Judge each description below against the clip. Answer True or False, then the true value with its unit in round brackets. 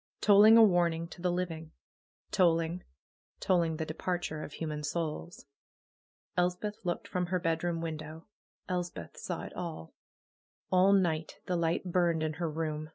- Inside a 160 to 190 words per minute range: False (150 wpm)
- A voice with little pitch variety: True (2.1 semitones)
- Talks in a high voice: False (170 Hz)